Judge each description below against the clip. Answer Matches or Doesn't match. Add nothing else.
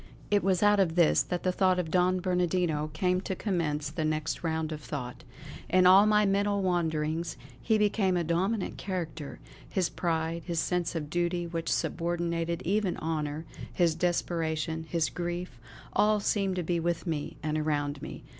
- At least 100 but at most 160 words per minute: Doesn't match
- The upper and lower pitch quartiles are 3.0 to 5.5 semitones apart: Doesn't match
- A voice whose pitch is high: Doesn't match